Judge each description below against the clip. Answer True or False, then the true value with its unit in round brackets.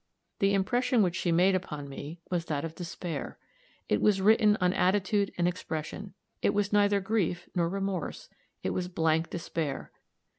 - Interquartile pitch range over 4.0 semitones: False (3.2 semitones)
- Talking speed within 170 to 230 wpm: False (160 wpm)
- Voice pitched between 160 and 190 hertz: True (185 Hz)